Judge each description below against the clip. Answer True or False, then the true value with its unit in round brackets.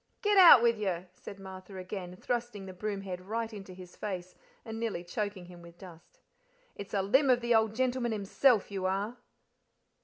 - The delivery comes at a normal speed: True (185 wpm)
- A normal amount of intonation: True (3.8 semitones)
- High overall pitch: True (200 Hz)